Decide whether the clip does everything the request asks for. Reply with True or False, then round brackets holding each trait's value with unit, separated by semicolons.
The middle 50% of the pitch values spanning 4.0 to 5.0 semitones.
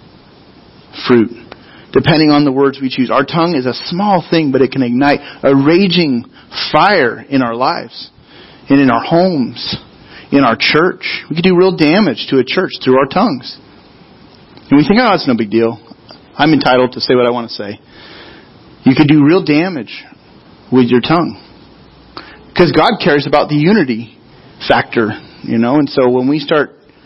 True (4.7 semitones)